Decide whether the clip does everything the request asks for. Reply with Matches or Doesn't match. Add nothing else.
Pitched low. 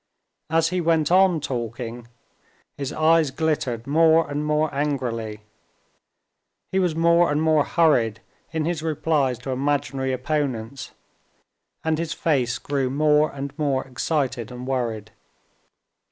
Doesn't match